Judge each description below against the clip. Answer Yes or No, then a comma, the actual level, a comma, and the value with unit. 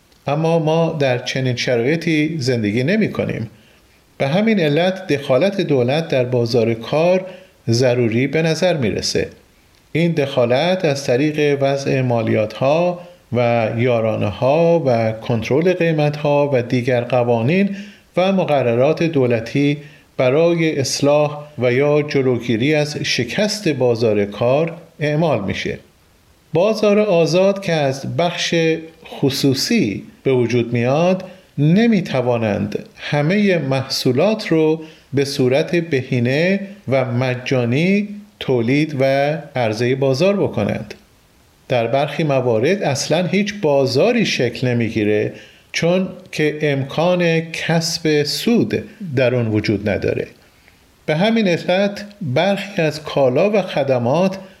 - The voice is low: No, medium, 145 Hz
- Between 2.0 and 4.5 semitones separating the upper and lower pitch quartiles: No, wide, 5.4 semitones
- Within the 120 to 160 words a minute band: No, average, 110 wpm